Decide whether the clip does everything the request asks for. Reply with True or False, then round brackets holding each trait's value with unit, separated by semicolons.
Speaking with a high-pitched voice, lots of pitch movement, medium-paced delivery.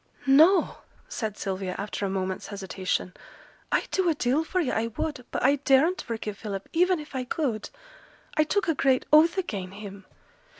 True (250 Hz; 7.8 semitones; 175 wpm)